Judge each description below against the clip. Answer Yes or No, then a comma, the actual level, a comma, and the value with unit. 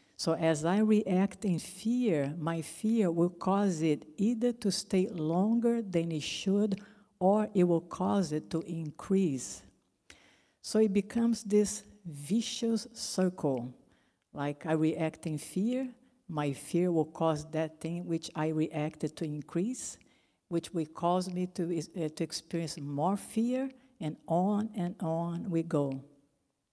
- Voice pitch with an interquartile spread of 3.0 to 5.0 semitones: Yes, average, 4.6 semitones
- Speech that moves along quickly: No, average, 140 wpm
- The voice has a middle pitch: Yes, medium, 175 Hz